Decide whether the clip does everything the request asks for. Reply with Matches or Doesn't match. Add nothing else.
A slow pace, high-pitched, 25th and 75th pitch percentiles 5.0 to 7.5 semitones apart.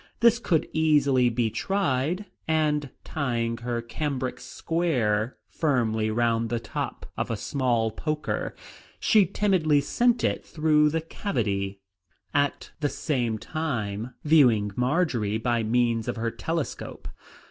Doesn't match